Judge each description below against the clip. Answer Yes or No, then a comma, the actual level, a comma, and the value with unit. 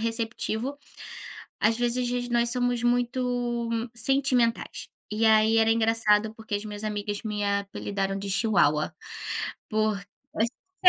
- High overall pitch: Yes, high, 225 Hz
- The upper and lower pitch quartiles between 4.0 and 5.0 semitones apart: No, narrow, 2.5 semitones